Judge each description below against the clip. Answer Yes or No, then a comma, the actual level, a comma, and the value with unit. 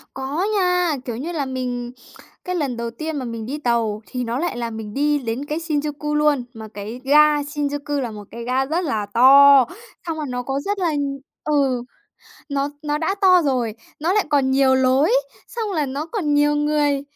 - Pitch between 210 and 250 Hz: No, very high, 280 Hz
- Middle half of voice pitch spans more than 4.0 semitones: No, average, 3.4 semitones